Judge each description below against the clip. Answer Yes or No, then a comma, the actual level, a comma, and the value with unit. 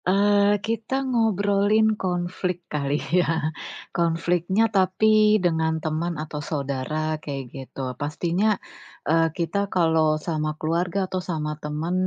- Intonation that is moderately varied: Yes, average, 4.2 semitones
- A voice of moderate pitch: Yes, medium, 170 Hz